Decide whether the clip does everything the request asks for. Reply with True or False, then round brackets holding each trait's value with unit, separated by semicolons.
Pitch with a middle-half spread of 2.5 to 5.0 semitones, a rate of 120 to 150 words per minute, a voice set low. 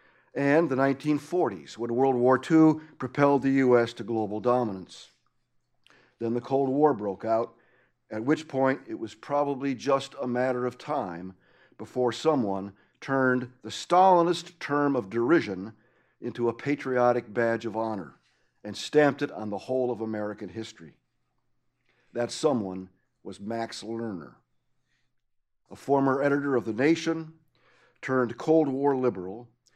True (4.0 semitones; 135 wpm; 125 Hz)